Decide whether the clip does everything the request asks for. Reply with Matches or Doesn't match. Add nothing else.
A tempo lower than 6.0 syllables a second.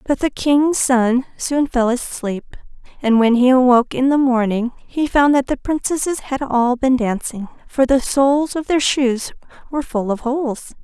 Matches